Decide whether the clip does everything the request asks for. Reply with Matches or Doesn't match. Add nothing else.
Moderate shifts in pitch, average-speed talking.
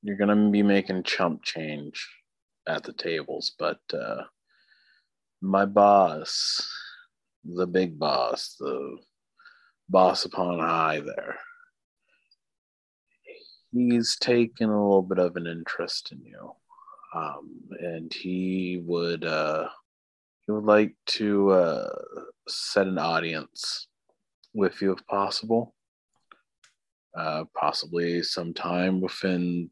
Doesn't match